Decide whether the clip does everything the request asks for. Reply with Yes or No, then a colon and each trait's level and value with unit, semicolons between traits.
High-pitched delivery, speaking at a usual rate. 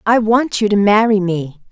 No: high, 205 Hz; fast, 210 wpm